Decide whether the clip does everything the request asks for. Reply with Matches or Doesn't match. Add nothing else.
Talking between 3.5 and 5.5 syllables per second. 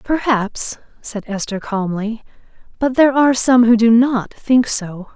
Matches